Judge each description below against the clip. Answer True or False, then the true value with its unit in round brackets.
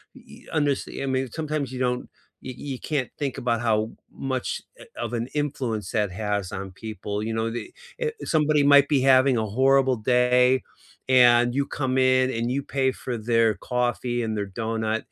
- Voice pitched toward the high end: False (125 Hz)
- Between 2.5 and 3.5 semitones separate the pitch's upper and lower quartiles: True (2.9 semitones)